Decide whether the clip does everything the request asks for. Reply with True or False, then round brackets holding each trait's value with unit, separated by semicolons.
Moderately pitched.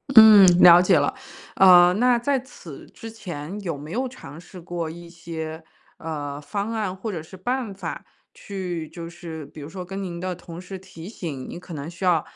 True (175 Hz)